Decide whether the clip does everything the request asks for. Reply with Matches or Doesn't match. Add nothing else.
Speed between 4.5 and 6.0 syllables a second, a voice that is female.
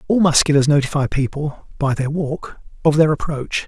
Doesn't match